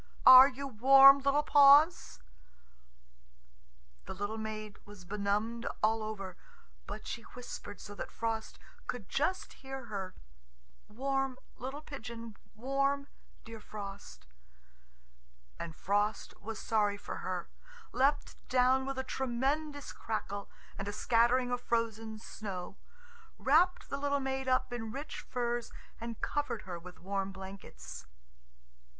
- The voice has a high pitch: Yes, high, 235 Hz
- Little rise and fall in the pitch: No, average, 4.6 semitones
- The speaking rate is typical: No, slow, 125 wpm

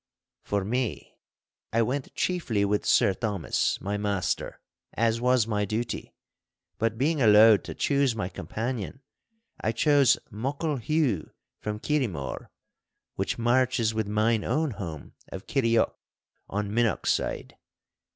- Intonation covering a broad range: No, average, 3.8 semitones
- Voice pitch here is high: No, low, 115 Hz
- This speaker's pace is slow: Yes, slow, 120 wpm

